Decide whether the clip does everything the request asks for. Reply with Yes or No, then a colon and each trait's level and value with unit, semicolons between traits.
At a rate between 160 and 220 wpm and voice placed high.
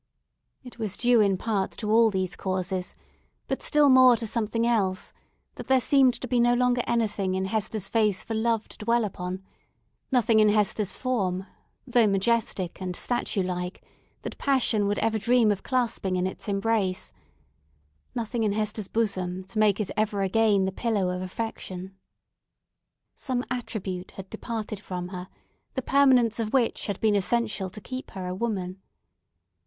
Yes: average, 165 wpm; high, 215 Hz